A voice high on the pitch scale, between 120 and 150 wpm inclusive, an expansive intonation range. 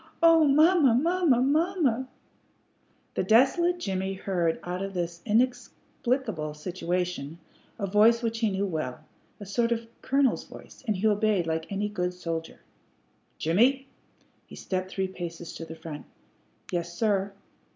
Yes: high, 200 Hz; average, 140 wpm; wide, 6.0 semitones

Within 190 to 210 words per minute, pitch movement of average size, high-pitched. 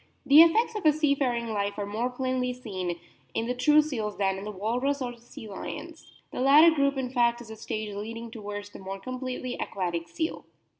Yes: fast, 205 wpm; average, 4.6 semitones; high, 240 Hz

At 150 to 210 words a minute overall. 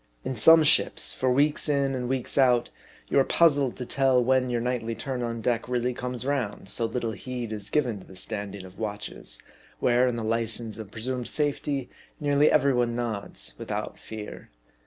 Yes: average, 185 wpm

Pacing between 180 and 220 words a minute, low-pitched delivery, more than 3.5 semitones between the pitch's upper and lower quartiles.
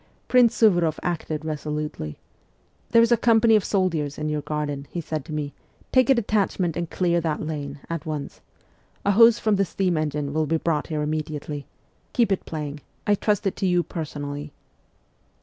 No: average, 185 wpm; medium, 160 Hz; average, 4.8 semitones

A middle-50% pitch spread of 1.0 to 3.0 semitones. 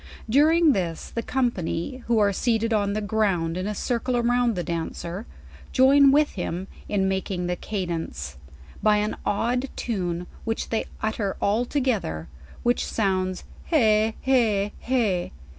No: average, 4.8 semitones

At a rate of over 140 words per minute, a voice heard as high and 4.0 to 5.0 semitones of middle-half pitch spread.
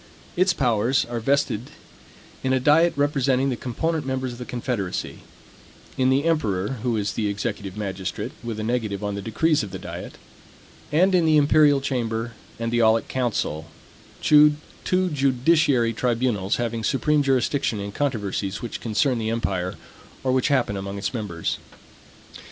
No: average, 155 wpm; low, 120 Hz; average, 4.7 semitones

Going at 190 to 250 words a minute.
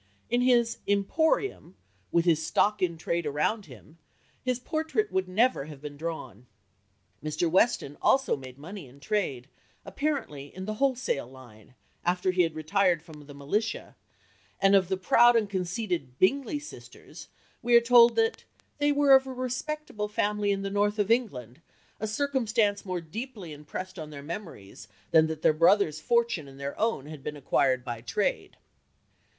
No: average, 165 wpm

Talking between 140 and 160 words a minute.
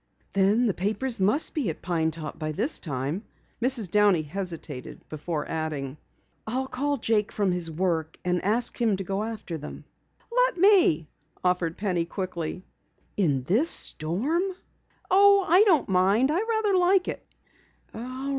Yes: average, 145 wpm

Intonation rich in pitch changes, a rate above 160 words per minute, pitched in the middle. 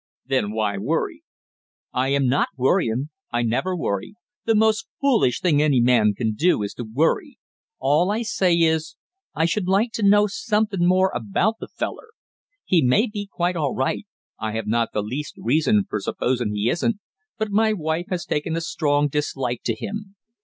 Yes: wide, 8.3 semitones; average, 180 wpm; medium, 155 Hz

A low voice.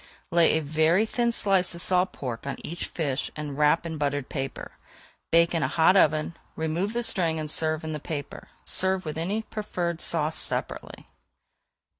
No: medium, 160 Hz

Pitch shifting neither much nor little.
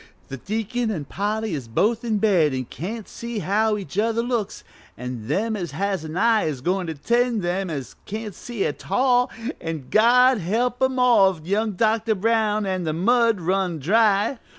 Yes: average, 4.6 semitones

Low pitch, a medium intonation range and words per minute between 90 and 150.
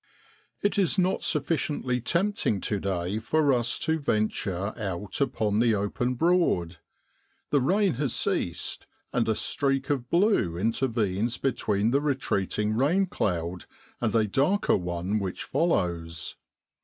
No: low, 115 Hz; wide, 6.6 semitones; slow, 135 wpm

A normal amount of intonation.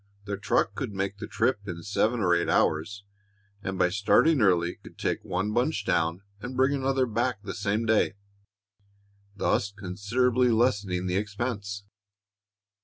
Yes: average, 4.0 semitones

